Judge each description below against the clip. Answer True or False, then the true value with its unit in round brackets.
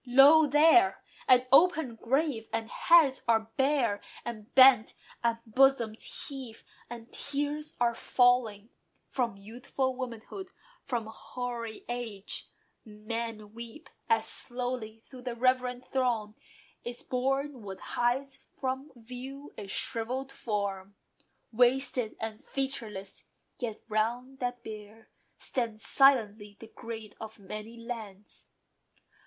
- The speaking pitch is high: True (240 Hz)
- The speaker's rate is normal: False (115 wpm)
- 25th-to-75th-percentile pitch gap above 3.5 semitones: False (3.2 semitones)